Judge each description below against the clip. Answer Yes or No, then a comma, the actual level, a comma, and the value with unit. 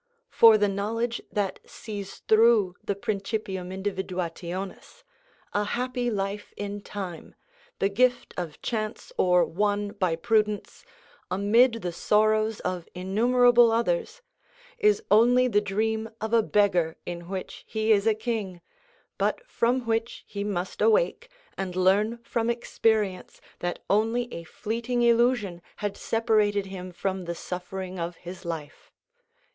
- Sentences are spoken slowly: Yes, slow, 130 wpm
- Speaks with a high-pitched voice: Yes, high, 210 Hz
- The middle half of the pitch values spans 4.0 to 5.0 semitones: No, average, 3.5 semitones